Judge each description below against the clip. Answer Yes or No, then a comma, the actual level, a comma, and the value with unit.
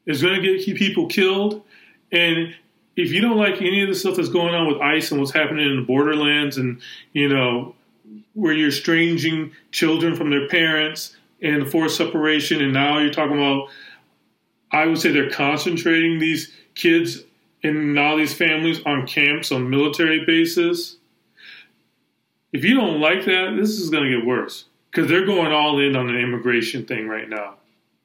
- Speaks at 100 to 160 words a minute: No, average, 175 wpm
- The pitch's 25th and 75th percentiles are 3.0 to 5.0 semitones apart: Yes, average, 3.6 semitones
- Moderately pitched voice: Yes, medium, 155 Hz